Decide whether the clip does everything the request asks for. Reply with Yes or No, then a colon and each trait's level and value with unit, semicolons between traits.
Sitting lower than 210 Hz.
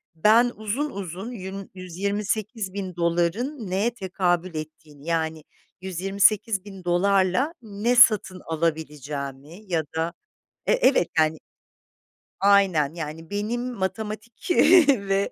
Yes: high, 190 Hz